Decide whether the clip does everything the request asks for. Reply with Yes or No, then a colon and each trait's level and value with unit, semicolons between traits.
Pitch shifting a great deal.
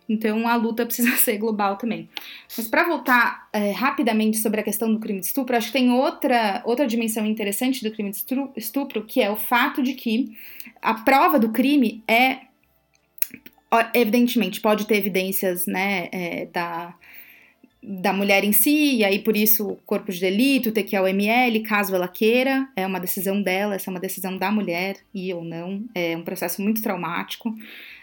No: average, 3.7 semitones